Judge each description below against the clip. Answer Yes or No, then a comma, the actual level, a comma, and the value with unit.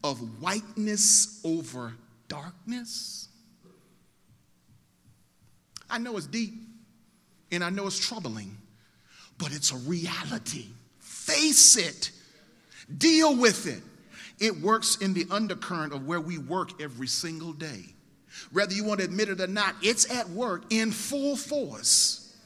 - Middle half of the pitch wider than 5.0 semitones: Yes, wide, 5.4 semitones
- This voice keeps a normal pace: No, slow, 130 wpm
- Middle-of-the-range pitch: No, high, 200 Hz